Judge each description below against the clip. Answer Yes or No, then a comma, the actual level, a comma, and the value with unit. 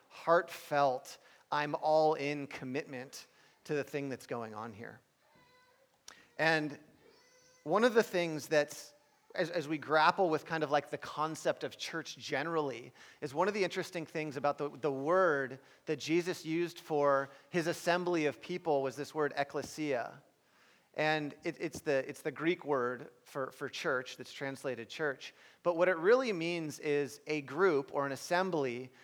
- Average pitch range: Yes, average, 3.4 semitones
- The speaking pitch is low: No, medium, 150 Hz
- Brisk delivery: No, average, 160 wpm